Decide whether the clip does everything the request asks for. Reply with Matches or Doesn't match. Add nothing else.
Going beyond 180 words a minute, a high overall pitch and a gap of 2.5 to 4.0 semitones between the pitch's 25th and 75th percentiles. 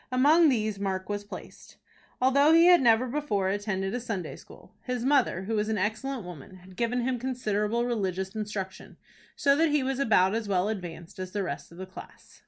Doesn't match